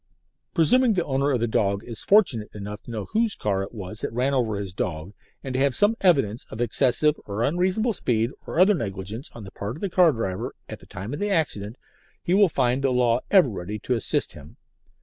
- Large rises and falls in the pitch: Yes, wide, 8.1 semitones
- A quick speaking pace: Yes, fast, 225 wpm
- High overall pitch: No, low, 120 Hz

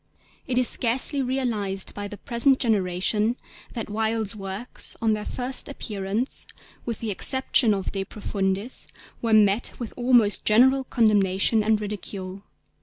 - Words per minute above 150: No, slow, 135 wpm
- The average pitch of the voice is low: No, high, 220 Hz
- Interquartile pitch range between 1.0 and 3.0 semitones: No, average, 3.5 semitones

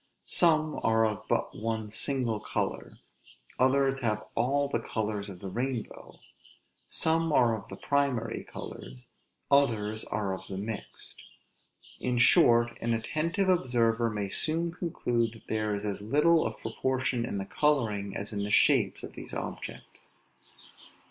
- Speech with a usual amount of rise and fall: Yes, average, 4.7 semitones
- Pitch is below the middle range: Yes, low, 115 Hz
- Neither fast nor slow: Yes, average, 145 wpm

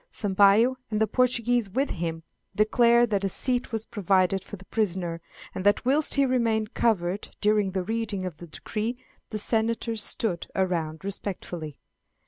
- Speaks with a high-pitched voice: Yes, high, 210 Hz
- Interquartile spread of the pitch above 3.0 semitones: Yes, average, 3.7 semitones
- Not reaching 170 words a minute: Yes, average, 155 wpm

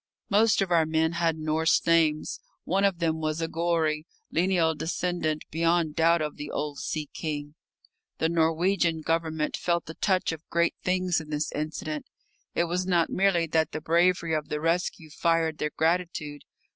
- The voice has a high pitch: No, medium, 165 Hz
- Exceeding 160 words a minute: Yes, average, 170 wpm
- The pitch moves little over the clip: Yes, narrow, 1.8 semitones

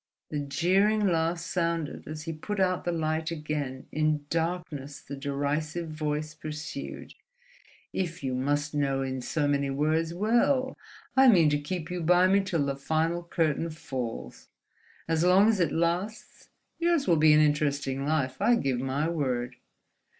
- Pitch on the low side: No, medium, 155 Hz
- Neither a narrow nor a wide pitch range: Yes, average, 3.4 semitones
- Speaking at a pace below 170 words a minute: Yes, average, 150 wpm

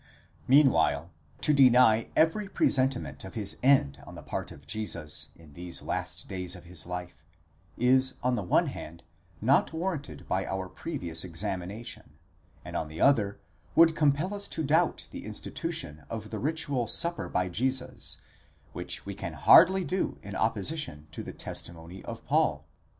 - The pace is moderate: Yes, average, 160 wpm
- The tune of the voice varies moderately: No, wide, 8.2 semitones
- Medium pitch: No, low, 110 Hz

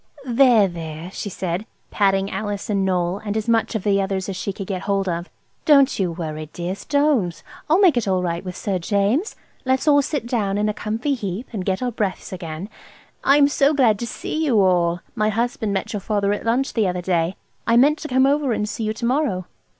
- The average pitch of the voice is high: Yes, high, 205 Hz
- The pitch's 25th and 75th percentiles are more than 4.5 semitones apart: Yes, average, 4.9 semitones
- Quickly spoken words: Yes, fast, 225 wpm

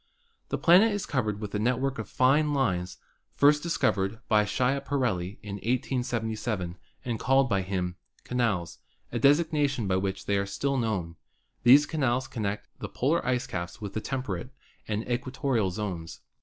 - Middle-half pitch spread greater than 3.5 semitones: Yes, average, 5.2 semitones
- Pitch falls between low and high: No, low, 115 Hz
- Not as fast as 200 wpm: Yes, average, 150 wpm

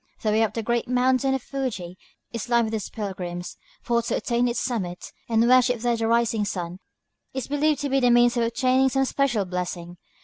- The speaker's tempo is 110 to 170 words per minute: No, fast, 205 wpm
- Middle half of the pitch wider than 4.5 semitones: No, average, 3.3 semitones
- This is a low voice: No, high, 235 Hz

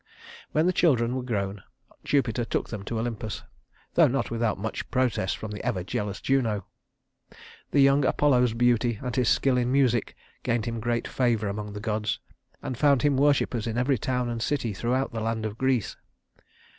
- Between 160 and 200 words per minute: Yes, average, 180 wpm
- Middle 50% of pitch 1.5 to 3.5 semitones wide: Yes, average, 3.1 semitones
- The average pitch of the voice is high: No, low, 120 Hz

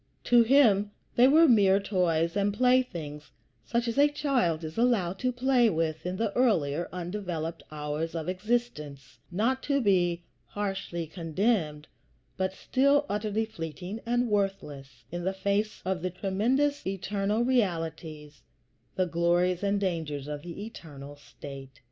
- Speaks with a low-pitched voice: No, high, 190 Hz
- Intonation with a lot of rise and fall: Yes, wide, 5.8 semitones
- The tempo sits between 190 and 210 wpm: No, average, 140 wpm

